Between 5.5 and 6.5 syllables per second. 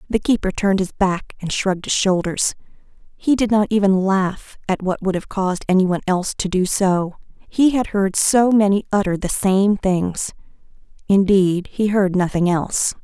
No: 4.9 syllables/s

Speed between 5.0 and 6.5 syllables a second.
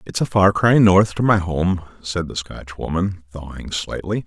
No: 4.4 syllables/s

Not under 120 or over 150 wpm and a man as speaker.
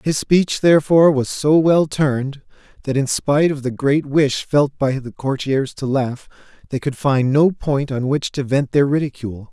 No: average, 195 wpm; male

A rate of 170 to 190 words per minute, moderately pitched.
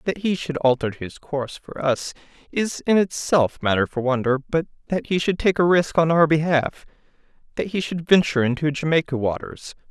Yes: average, 180 wpm; medium, 155 Hz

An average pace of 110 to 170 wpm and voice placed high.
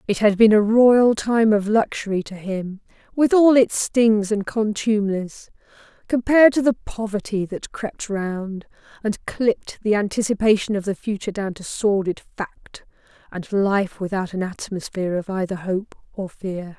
Yes: average, 155 wpm; high, 205 Hz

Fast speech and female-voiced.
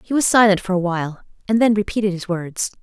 Yes: fast, 215 wpm; female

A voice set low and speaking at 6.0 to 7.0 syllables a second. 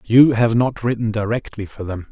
No: low, 115 Hz; 5.0 syllables/s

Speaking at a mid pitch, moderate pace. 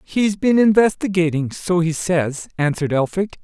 No: medium, 175 Hz; slow, 120 wpm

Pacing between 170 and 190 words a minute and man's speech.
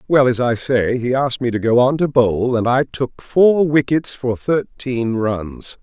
No: fast, 205 wpm; male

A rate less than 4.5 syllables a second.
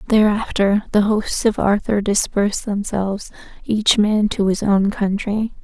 Yes: 4.3 syllables/s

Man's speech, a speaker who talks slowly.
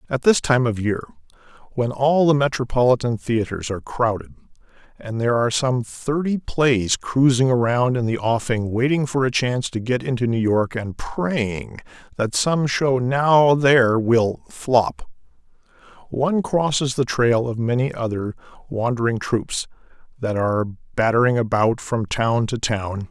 No: male; average, 150 wpm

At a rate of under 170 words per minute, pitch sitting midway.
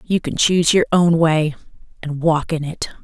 No: average, 200 wpm; medium, 160 Hz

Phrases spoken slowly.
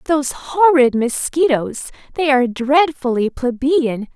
Yes: slow, 85 wpm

